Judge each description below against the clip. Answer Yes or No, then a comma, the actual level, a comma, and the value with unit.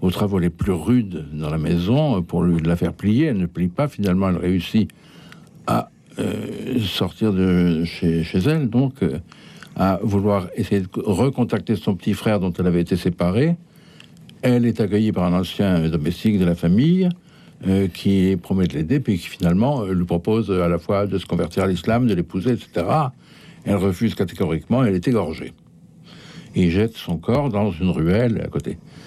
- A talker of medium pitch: No, low, 100 Hz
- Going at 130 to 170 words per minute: No, average, 180 wpm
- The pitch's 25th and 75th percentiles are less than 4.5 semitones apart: No, wide, 5.4 semitones